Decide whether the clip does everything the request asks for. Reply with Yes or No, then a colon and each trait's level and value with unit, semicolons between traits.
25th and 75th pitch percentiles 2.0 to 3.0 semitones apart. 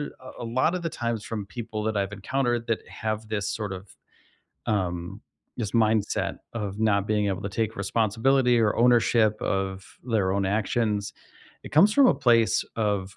Yes: average, 2.7 semitones